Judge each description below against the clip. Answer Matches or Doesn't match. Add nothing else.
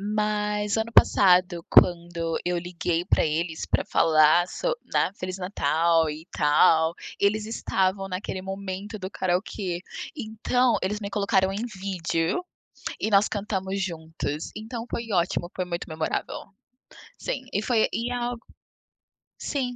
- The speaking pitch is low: Doesn't match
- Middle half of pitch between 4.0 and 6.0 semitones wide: Doesn't match